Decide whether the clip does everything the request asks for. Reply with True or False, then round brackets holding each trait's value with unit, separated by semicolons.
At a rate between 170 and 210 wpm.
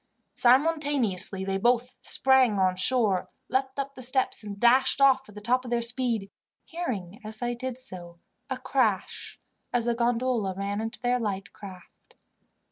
False (155 wpm)